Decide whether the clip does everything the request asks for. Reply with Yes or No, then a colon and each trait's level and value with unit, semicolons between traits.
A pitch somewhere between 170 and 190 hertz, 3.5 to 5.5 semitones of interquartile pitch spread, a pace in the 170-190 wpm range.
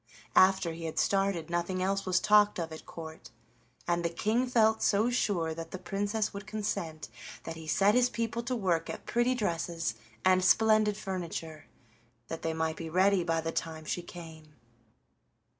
Yes: medium, 185 Hz; average, 4.2 semitones; average, 175 wpm